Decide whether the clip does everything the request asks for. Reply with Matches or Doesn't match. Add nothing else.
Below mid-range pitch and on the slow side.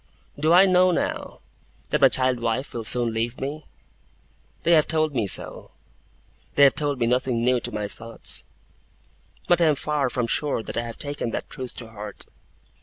Doesn't match